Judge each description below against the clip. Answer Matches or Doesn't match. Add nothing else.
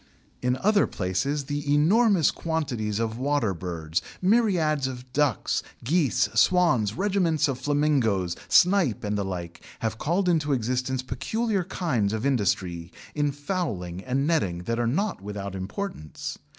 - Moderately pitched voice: Doesn't match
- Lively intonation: Matches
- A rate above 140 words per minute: Doesn't match